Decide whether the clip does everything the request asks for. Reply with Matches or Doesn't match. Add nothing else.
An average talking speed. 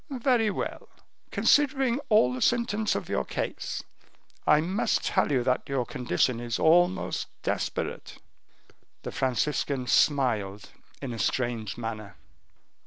Doesn't match